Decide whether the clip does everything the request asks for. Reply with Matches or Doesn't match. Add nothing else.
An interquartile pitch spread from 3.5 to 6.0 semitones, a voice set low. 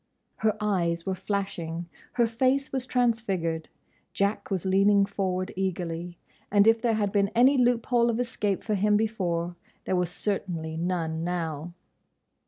Doesn't match